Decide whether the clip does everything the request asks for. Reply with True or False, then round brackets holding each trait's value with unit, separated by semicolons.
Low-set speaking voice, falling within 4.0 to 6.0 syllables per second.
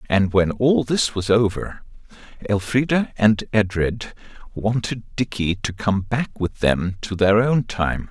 False (110 Hz; 3.8 syllables/s)